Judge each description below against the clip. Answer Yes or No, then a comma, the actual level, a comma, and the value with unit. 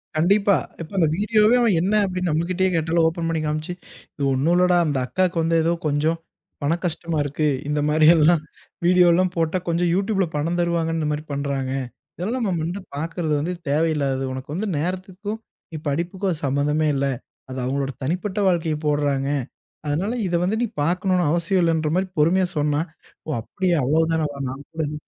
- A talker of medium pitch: Yes, medium, 165 Hz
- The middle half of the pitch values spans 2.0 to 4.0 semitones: Yes, average, 3.4 semitones